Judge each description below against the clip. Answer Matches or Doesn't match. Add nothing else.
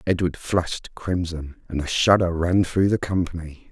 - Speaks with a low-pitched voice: Matches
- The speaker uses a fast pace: Doesn't match